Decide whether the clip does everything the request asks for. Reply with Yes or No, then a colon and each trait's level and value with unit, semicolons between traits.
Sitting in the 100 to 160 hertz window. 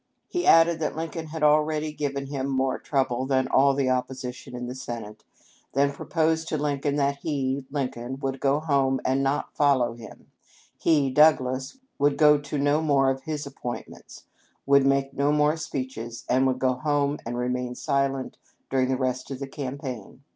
Yes: medium, 140 Hz